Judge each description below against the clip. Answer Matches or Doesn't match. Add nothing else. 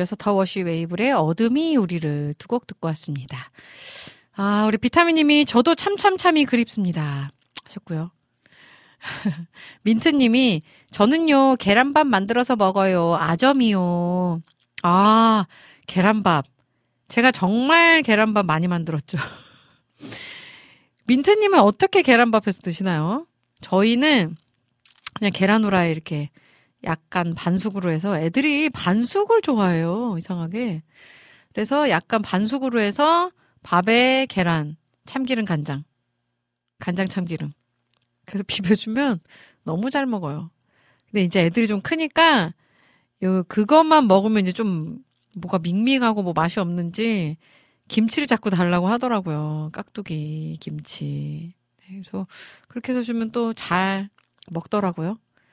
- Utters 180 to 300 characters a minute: Matches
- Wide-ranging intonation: Matches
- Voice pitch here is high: Matches